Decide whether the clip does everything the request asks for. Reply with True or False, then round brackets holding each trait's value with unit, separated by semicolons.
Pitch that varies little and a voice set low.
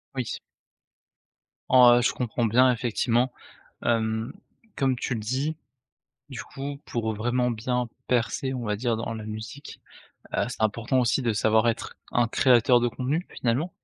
True (2.3 semitones; 120 Hz)